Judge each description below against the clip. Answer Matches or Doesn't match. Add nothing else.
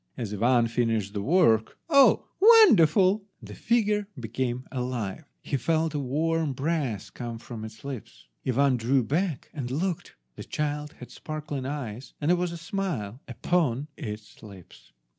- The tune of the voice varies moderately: Doesn't match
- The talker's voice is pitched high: Doesn't match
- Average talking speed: Matches